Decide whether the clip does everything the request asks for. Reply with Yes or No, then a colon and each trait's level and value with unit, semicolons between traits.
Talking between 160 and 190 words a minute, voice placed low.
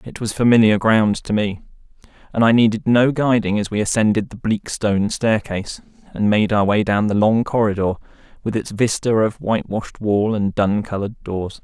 Yes: average, 185 wpm; low, 105 Hz